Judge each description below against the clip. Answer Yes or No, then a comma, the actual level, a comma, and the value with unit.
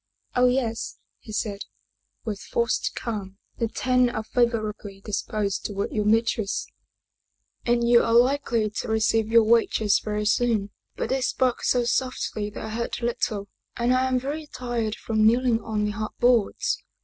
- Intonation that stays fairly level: Yes, narrow, 2.3 semitones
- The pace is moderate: Yes, average, 165 wpm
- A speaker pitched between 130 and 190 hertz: No, high, 225 Hz